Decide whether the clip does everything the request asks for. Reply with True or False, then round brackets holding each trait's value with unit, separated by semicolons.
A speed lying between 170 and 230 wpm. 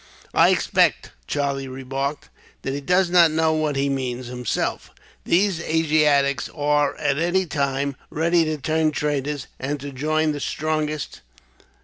False (140 wpm)